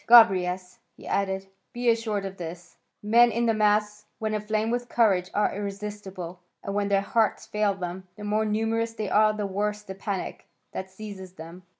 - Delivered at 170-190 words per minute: Yes, average, 180 wpm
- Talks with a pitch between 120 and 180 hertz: No, high, 210 Hz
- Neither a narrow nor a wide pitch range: No, narrow, 2.1 semitones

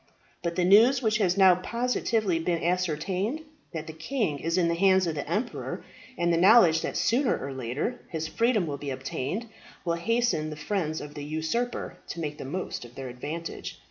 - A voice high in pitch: No, medium, 170 Hz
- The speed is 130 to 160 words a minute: No, average, 195 wpm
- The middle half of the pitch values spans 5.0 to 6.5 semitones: Yes, wide, 5.4 semitones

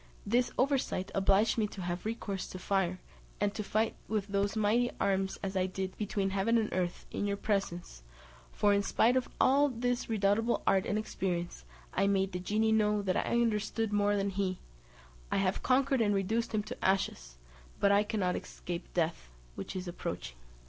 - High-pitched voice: Yes, high, 200 Hz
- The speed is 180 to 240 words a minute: Yes, average, 185 wpm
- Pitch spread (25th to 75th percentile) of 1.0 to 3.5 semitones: Yes, narrow, 2.6 semitones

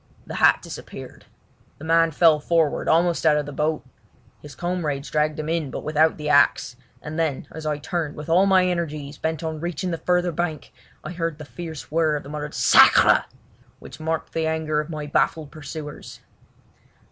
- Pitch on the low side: No, medium, 155 Hz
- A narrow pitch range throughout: Yes, narrow, 1.8 semitones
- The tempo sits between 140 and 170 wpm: No, average, 185 wpm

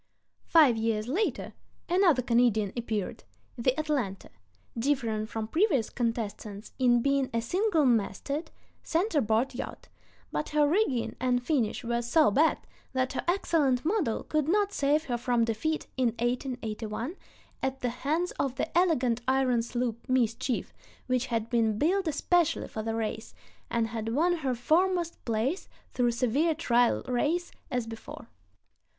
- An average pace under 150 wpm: Yes, average, 140 wpm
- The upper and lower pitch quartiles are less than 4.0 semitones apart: No, average, 5.0 semitones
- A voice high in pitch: Yes, very high, 250 Hz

